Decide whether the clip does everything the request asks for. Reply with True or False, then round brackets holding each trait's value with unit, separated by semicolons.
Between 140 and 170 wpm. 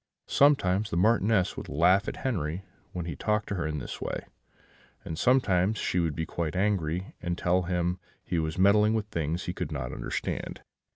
False (190 wpm)